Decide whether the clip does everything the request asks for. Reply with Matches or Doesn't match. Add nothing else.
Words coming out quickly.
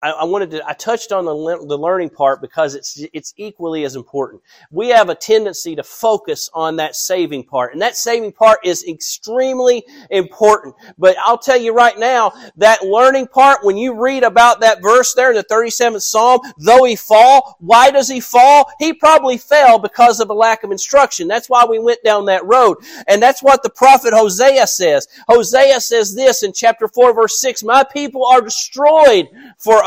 Doesn't match